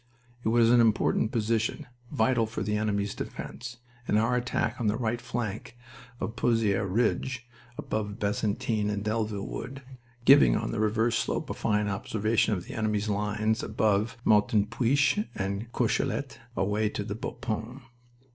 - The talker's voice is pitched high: No, low, 110 Hz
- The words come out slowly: No, average, 145 wpm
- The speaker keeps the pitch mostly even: Yes, narrow, 2.2 semitones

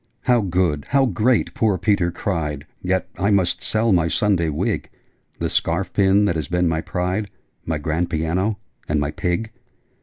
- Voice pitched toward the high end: No, very low, 90 Hz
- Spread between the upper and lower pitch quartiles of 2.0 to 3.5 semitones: No, average, 3.9 semitones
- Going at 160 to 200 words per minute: Yes, average, 170 wpm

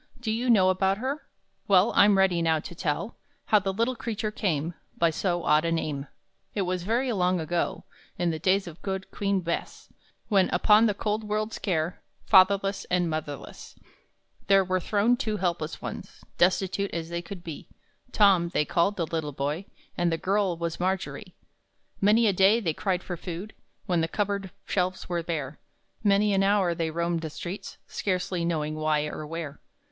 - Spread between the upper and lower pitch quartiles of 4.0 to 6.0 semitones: No, average, 3.2 semitones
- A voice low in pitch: No, medium, 185 Hz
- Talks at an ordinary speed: Yes, average, 180 wpm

